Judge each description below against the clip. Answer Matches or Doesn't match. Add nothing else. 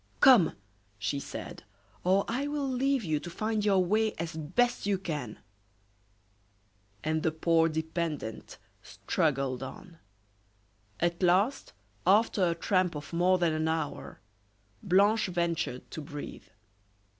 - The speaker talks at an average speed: Doesn't match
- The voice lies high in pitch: Doesn't match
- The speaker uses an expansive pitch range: Doesn't match